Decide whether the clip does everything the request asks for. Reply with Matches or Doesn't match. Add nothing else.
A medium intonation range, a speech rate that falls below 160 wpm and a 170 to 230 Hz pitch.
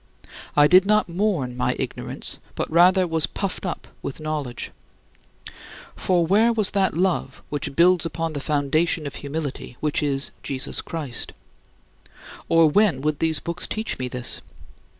Doesn't match